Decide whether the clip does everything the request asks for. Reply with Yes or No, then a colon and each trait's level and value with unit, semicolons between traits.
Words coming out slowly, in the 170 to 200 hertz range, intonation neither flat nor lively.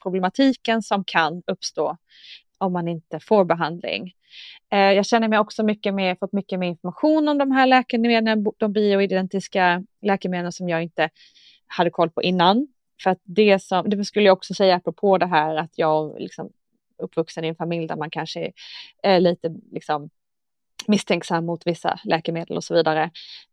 No: average, 170 wpm; medium, 185 Hz; average, 3.8 semitones